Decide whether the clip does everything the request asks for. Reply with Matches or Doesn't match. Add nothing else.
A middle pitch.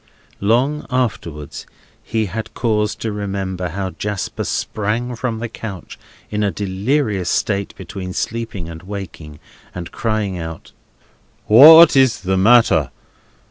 Doesn't match